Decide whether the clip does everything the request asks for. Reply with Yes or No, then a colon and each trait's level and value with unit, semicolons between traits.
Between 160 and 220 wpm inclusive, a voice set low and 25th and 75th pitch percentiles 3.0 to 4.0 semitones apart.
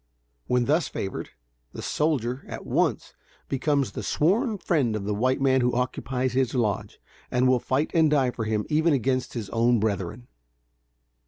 Yes: average, 165 wpm; low, 130 Hz; average, 3.7 semitones